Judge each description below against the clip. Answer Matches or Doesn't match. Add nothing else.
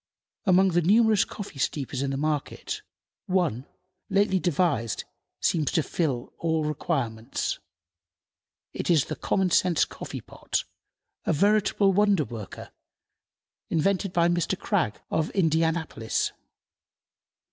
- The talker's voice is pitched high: Doesn't match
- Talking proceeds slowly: Matches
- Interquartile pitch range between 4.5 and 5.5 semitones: Matches